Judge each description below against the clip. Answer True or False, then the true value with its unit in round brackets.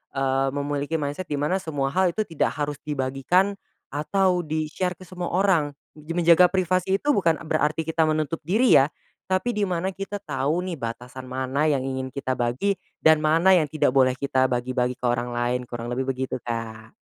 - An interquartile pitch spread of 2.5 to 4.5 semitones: False (5.3 semitones)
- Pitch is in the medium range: True (150 Hz)